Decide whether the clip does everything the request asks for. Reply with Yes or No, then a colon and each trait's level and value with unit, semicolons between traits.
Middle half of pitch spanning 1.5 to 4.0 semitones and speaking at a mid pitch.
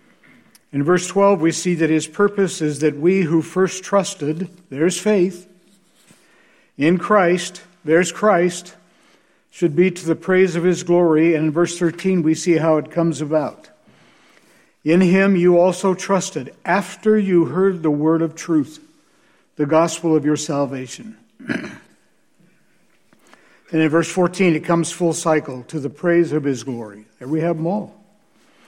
Yes: average, 2.9 semitones; medium, 170 Hz